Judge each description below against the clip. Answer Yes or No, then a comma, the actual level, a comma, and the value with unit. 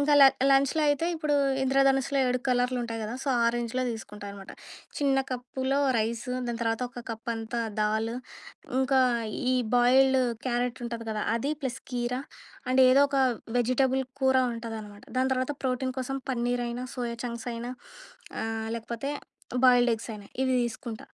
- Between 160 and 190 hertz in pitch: No, high, 245 Hz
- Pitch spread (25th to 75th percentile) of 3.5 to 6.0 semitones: No, narrow, 2.4 semitones